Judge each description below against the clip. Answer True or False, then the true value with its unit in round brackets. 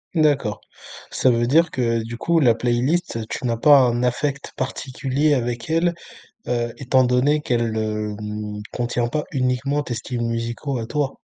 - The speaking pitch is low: True (125 Hz)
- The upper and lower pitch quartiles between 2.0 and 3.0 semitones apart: False (3.4 semitones)